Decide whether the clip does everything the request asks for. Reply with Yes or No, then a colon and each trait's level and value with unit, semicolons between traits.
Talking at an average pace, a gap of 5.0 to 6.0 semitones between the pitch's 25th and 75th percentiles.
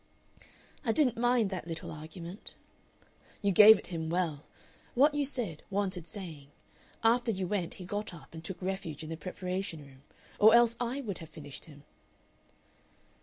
Yes: average, 165 wpm; average, 5.3 semitones